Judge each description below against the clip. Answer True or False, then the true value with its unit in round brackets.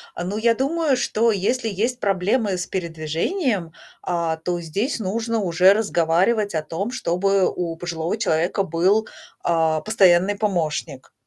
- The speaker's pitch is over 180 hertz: True (190 Hz)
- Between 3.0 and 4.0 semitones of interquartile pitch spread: False (4.6 semitones)